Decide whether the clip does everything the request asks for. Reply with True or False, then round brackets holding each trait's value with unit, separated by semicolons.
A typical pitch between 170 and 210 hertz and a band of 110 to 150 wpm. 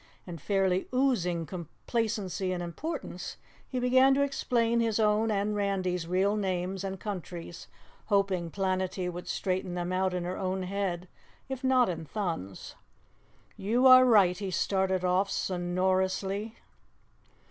True (190 Hz; 135 wpm)